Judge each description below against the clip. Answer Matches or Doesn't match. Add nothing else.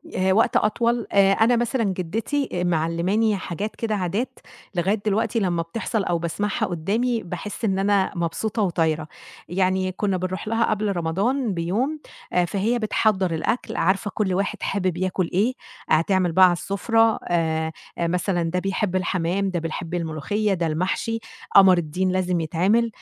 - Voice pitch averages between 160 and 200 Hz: Matches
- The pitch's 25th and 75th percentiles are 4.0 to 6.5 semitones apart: Doesn't match